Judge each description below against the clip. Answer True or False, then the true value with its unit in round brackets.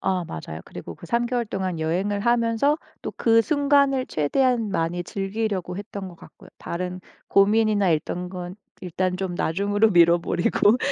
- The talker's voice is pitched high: True (195 Hz)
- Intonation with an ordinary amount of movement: True (4.3 semitones)